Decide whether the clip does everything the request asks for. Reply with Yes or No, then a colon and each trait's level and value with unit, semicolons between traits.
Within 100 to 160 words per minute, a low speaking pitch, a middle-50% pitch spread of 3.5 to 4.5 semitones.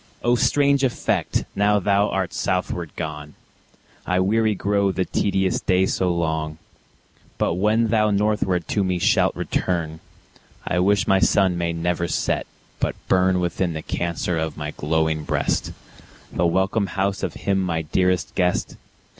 No: average, 150 wpm; very low, 90 Hz; average, 2.9 semitones